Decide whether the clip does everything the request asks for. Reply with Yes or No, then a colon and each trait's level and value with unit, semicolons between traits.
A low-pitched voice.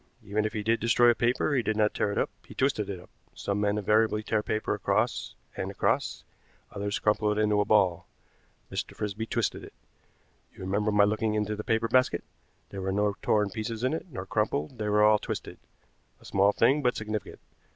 Yes: low, 105 Hz